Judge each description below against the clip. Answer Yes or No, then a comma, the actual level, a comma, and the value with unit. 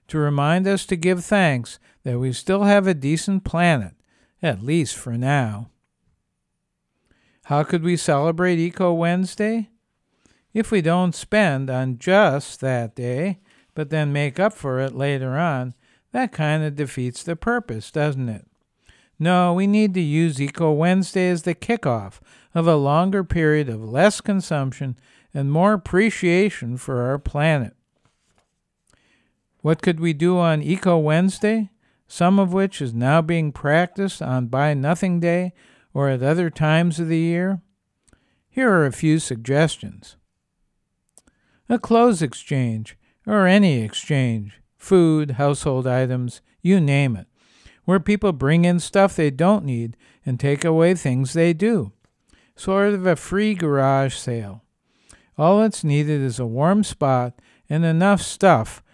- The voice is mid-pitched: Yes, medium, 160 Hz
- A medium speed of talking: Yes, average, 145 wpm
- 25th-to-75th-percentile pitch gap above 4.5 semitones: Yes, wide, 5.6 semitones